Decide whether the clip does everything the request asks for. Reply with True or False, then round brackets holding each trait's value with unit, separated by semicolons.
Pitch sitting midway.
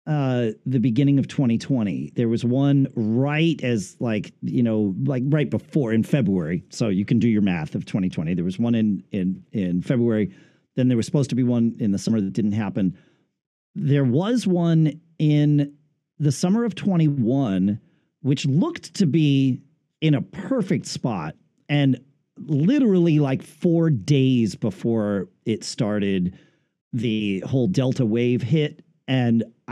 False (130 Hz)